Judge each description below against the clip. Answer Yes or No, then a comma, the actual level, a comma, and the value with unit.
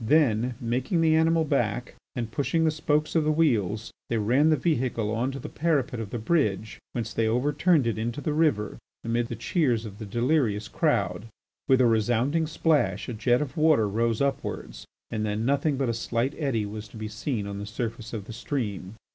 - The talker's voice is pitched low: Yes, low, 120 Hz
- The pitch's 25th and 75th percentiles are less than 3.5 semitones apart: No, average, 5.2 semitones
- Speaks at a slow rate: No, average, 200 wpm